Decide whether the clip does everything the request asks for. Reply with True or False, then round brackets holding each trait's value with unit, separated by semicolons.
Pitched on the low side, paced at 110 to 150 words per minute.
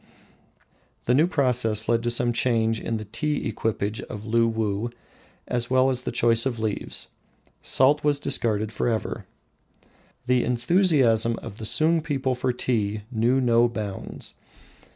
True (120 Hz; 145 wpm)